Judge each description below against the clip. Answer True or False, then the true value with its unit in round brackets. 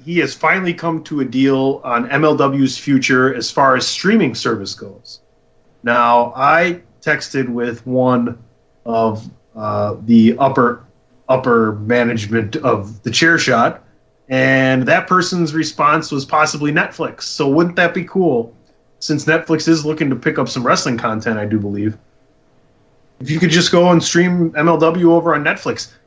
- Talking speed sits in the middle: True (155 wpm)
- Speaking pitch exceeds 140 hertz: False (135 Hz)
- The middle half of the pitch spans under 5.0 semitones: False (5.4 semitones)